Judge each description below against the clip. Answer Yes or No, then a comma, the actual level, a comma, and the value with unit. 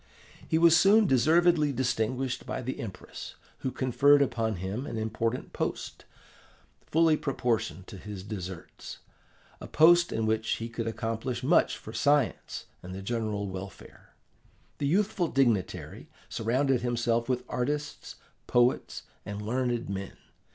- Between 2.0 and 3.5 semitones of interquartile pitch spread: No, average, 4.4 semitones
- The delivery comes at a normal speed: No, slow, 130 wpm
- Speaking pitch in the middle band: No, low, 120 Hz